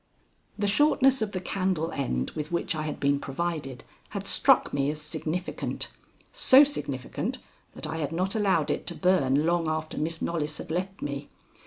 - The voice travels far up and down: No, average, 4.2 semitones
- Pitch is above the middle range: No, medium, 160 Hz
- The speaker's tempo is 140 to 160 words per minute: No, average, 175 wpm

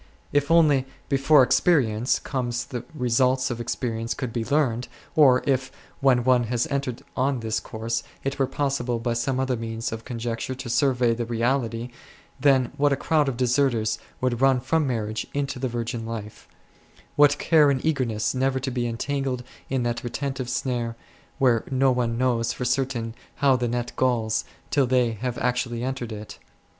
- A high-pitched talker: No, low, 125 Hz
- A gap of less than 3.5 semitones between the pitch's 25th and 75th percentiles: Yes, narrow, 2.4 semitones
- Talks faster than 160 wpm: Yes, average, 170 wpm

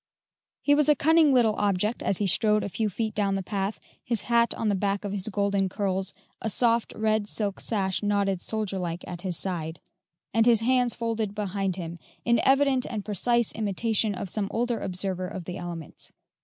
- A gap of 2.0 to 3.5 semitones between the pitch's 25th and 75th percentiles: Yes, average, 3.1 semitones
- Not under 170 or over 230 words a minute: Yes, average, 195 wpm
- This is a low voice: No, high, 205 Hz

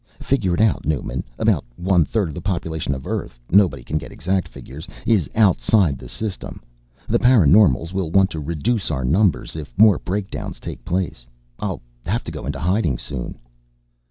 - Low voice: Yes, very low, 90 Hz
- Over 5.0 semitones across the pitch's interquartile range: Yes, wide, 5.4 semitones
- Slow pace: No, average, 170 wpm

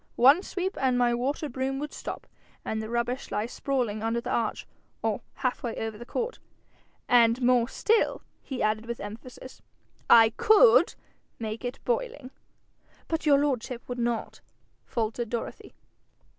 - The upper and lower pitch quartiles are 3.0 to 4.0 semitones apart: Yes, average, 3.3 semitones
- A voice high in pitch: Yes, high, 245 Hz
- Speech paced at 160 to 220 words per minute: No, average, 150 wpm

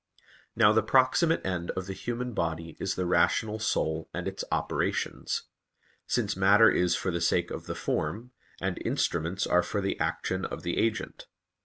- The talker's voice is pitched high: No, very low, 95 Hz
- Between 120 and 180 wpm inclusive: Yes, average, 170 wpm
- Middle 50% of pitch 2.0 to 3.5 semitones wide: No, average, 4.2 semitones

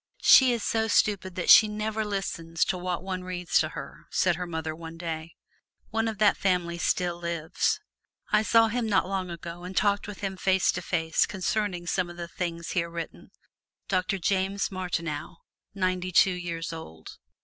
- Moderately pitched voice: Yes, medium, 180 Hz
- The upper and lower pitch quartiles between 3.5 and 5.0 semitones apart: No, average, 2.8 semitones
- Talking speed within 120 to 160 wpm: No, average, 180 wpm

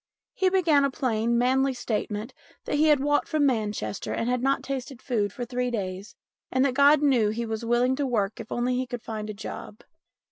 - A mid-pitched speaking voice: No, high, 245 Hz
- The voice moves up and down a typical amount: Yes, average, 3.8 semitones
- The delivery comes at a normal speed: No, fast, 210 wpm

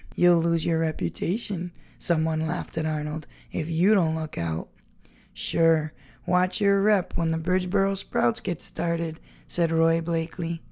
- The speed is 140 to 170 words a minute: Yes, average, 145 wpm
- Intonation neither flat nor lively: No, narrow, 2.0 semitones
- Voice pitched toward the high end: No, medium, 165 Hz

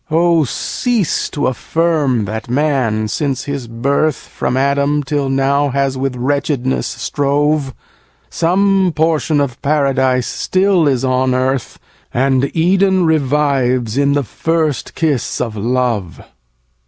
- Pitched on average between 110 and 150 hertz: Yes, medium, 140 Hz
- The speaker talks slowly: Yes, slow, 125 wpm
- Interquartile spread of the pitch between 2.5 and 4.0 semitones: Yes, average, 3.3 semitones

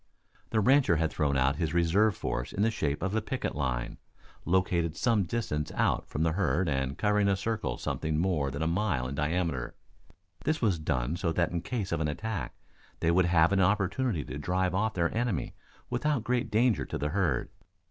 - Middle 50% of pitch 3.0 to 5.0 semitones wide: No, wide, 5.5 semitones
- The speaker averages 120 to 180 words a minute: No, average, 200 wpm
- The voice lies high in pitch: No, very low, 85 Hz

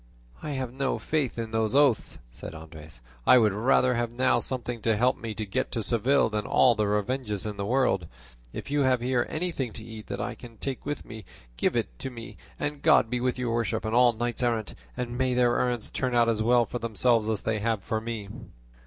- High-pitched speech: No, low, 120 Hz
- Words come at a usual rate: No, fast, 225 wpm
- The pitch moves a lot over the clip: No, narrow, 2.6 semitones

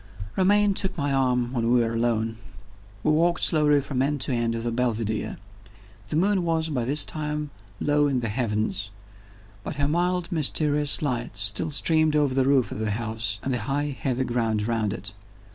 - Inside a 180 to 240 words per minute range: Yes, average, 185 wpm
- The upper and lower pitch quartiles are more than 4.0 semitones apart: Yes, average, 4.6 semitones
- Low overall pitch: Yes, low, 130 Hz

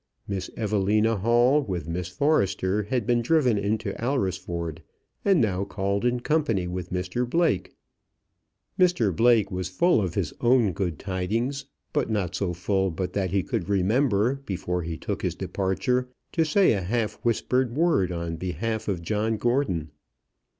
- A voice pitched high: No, low, 100 Hz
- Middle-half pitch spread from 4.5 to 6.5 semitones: Yes, average, 4.9 semitones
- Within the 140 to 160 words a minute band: Yes, average, 155 wpm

